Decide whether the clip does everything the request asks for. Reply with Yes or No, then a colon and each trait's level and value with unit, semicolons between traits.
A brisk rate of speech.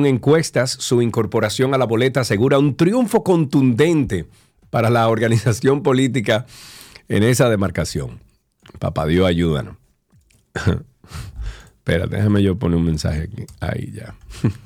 No: slow, 125 wpm